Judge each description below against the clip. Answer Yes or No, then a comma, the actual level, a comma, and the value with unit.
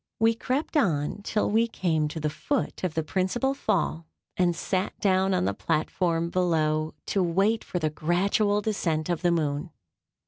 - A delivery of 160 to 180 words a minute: Yes, average, 165 wpm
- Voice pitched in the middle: Yes, medium, 180 Hz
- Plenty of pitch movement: No, average, 4.5 semitones